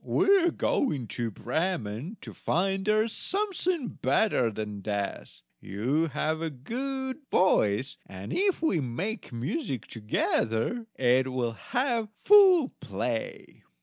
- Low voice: No, medium, 160 Hz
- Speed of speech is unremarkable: No, slow, 120 wpm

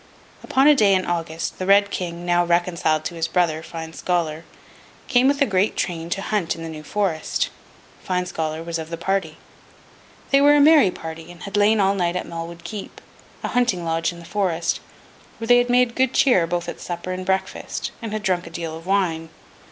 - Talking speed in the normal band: No, fast, 210 wpm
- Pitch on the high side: No, medium, 175 Hz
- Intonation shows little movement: No, average, 3.6 semitones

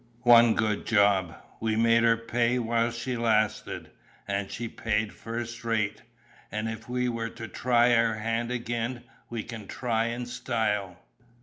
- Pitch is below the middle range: Yes, low, 115 Hz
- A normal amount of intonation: No, narrow, 1.3 semitones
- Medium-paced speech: Yes, average, 150 wpm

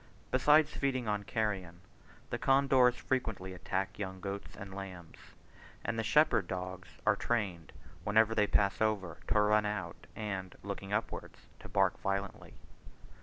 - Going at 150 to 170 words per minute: No, average, 140 wpm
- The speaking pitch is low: Yes, low, 100 Hz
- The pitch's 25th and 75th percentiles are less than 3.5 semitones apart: Yes, average, 2.9 semitones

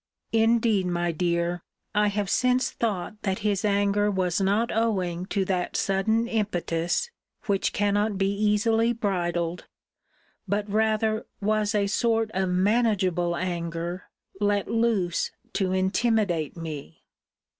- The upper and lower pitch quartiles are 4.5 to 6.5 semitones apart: No, average, 3.3 semitones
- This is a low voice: No, high, 200 Hz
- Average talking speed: No, slow, 120 wpm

